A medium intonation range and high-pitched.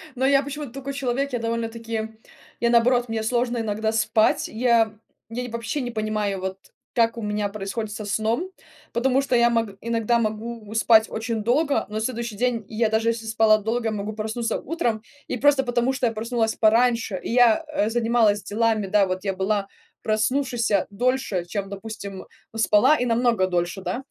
No: narrow, 2.1 semitones; high, 225 Hz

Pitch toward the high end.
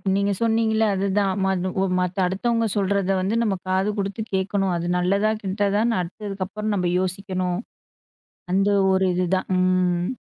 Yes: high, 195 Hz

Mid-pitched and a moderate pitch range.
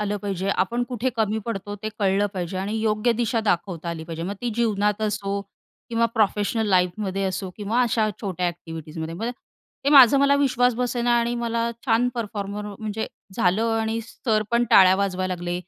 No: high, 210 Hz; average, 3.6 semitones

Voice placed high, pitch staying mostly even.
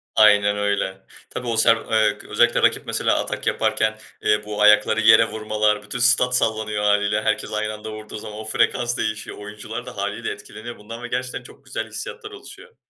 No: low, 110 Hz; narrow, 1.6 semitones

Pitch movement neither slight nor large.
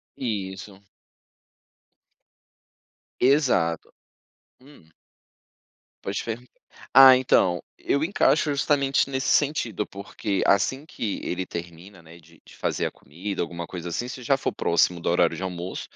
No: wide, 7.2 semitones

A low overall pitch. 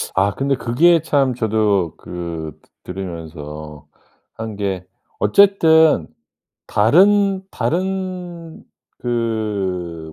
Yes: low, 110 Hz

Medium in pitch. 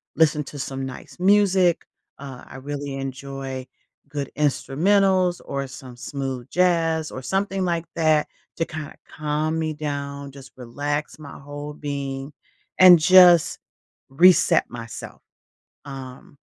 Yes: medium, 145 Hz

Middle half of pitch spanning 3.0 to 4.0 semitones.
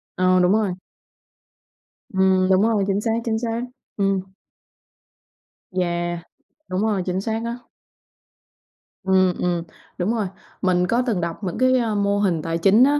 Yes: average, 3.3 semitones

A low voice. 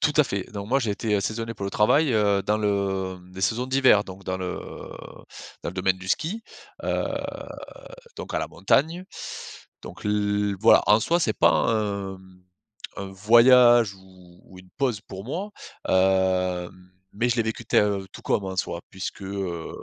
Yes: low, 100 Hz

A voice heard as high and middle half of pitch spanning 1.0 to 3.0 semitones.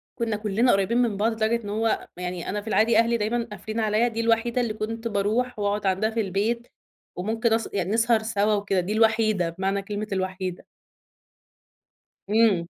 Yes: high, 215 Hz; narrow, 2.4 semitones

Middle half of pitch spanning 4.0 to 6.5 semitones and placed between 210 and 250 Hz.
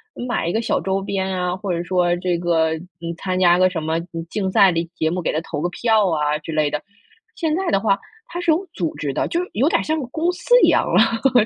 No: average, 5.3 semitones; medium, 185 Hz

